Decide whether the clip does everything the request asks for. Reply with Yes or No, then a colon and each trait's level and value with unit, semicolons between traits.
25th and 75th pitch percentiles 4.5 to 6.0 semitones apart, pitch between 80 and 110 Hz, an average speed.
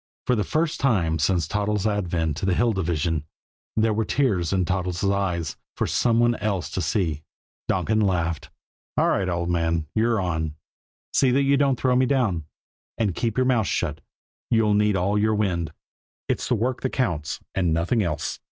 Yes: average, 5.0 semitones; low, 100 Hz; average, 180 wpm